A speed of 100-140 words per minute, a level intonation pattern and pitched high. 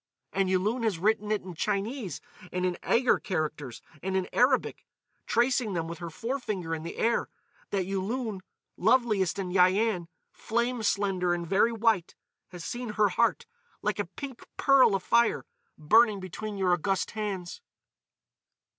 No: slow, 135 wpm; average, 4.0 semitones; high, 200 Hz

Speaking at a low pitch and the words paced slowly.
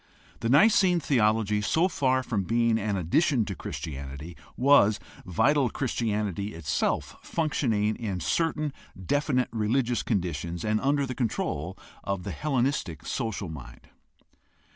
Yes: low, 110 Hz; slow, 120 wpm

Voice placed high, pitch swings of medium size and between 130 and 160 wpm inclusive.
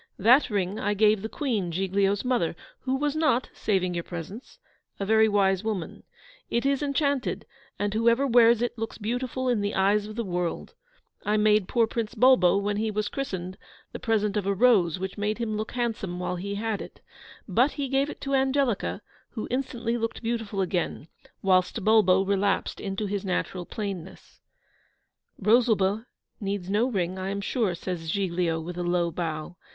No: high, 210 Hz; average, 3.8 semitones; average, 175 wpm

